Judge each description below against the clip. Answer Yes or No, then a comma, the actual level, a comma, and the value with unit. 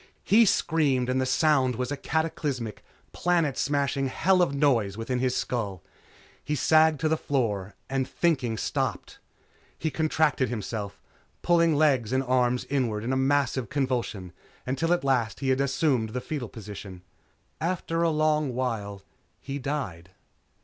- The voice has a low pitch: Yes, low, 130 Hz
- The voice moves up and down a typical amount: Yes, average, 4.4 semitones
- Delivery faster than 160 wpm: No, average, 150 wpm